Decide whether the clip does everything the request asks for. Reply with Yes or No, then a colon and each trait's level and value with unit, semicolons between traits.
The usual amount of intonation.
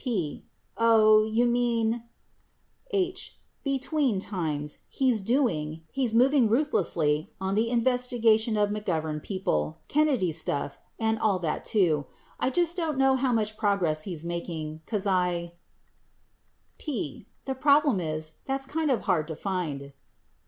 No: wide, 7.2 semitones